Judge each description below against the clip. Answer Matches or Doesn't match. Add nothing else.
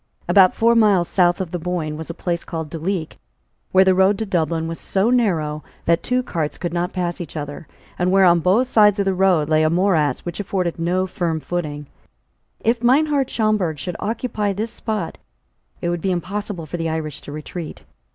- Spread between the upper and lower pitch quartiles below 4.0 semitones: Matches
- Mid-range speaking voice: Matches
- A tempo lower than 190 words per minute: Doesn't match